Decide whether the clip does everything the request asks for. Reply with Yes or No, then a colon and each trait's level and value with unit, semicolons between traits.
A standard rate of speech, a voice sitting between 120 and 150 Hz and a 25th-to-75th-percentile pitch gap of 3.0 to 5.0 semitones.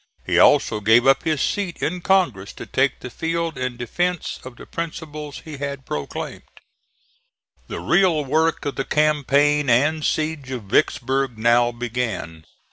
Yes: average, 150 wpm; medium, 140 Hz; average, 4.5 semitones